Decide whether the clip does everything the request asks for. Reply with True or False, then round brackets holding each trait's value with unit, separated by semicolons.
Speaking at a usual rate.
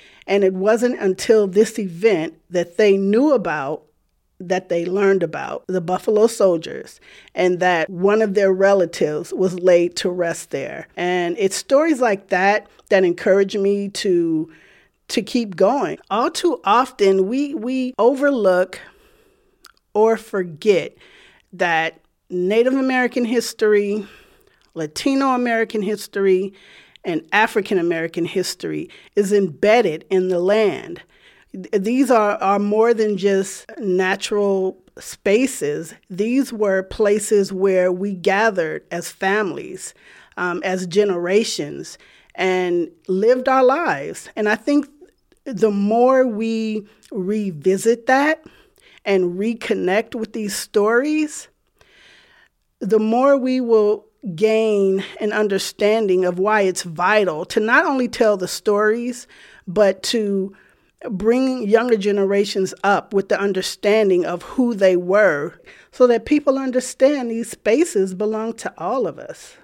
False (120 wpm)